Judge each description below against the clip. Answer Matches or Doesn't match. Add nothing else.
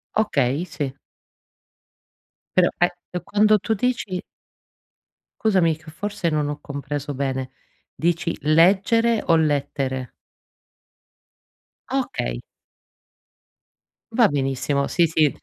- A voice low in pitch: Doesn't match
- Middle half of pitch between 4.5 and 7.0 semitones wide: Matches